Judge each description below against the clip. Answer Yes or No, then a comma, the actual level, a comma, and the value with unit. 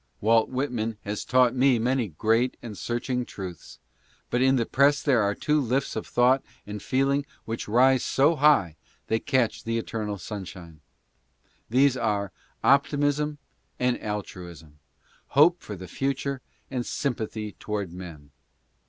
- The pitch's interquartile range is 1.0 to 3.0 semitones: No, average, 4.4 semitones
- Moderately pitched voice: No, low, 120 Hz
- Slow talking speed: No, average, 145 wpm